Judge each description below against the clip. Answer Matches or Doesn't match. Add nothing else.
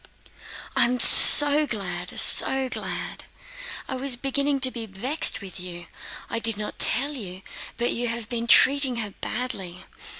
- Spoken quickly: Doesn't match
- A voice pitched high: Matches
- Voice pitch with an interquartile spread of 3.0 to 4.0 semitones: Doesn't match